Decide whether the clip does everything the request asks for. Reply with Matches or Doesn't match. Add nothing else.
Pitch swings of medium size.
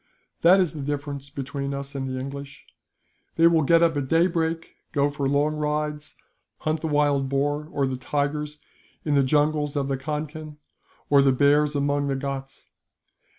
Doesn't match